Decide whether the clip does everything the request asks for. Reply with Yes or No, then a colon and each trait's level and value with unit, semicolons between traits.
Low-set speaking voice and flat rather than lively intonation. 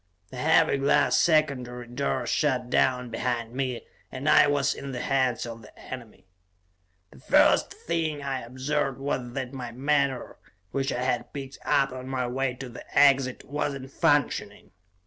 Yes: low, 130 Hz; narrow, 2.1 semitones